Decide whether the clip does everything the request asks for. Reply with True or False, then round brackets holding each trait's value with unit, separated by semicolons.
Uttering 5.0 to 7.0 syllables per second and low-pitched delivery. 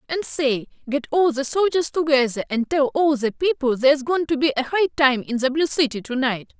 False (5.2 syllables/s; 280 Hz)